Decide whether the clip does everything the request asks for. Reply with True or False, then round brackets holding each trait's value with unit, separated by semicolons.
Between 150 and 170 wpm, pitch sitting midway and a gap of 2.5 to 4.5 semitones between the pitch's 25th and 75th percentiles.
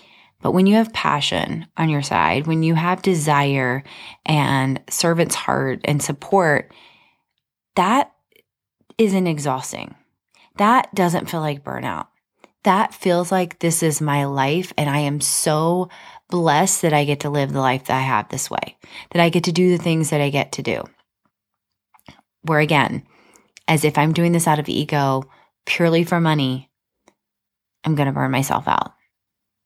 True (160 wpm; 155 Hz; 3.8 semitones)